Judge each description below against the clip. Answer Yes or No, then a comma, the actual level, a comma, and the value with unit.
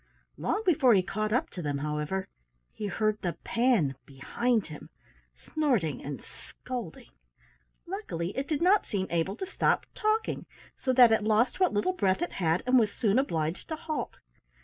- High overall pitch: Yes, high, 215 Hz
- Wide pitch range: Yes, wide, 7.6 semitones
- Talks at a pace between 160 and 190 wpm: Yes, average, 170 wpm